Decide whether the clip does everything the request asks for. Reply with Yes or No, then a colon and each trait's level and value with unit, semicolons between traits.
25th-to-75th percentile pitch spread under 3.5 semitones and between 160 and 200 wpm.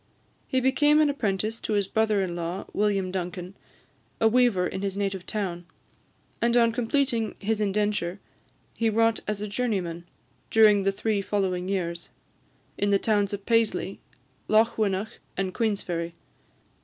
No: average, 2.9 semitones; average, 145 wpm